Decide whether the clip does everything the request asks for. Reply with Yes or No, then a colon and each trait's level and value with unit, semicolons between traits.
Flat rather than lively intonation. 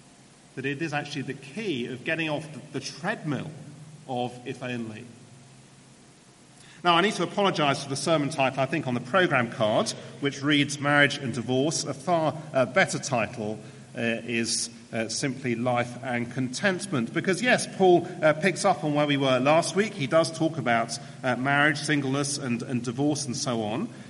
No: average, 3.9 semitones